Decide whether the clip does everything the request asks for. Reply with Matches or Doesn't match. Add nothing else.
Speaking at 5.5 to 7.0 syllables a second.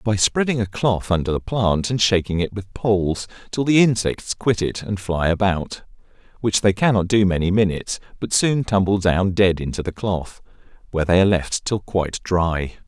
Doesn't match